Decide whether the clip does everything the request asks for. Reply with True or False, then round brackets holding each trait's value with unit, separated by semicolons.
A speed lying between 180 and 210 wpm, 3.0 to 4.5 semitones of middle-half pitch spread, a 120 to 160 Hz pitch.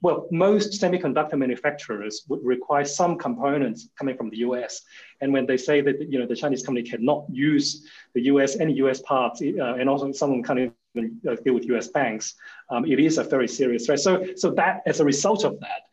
True (205 wpm; 3.3 semitones; 140 Hz)